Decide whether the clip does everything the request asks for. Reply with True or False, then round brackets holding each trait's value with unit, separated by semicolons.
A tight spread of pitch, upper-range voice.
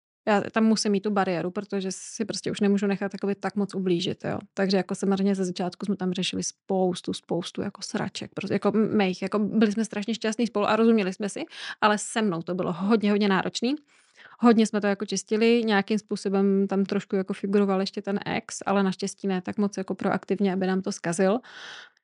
True (1.9 semitones; 200 Hz)